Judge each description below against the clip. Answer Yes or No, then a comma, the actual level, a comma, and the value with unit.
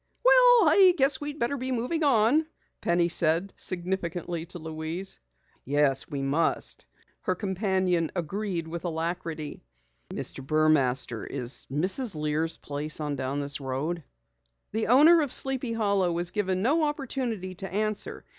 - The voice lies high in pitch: No, medium, 180 Hz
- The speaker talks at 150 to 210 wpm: No, slow, 135 wpm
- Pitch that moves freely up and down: Yes, wide, 7.0 semitones